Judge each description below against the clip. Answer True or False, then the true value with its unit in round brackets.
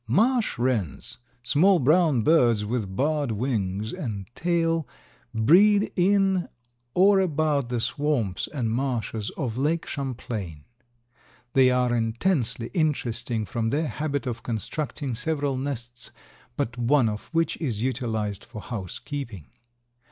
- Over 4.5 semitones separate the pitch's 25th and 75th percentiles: True (5.6 semitones)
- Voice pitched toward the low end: True (130 Hz)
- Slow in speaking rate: True (120 wpm)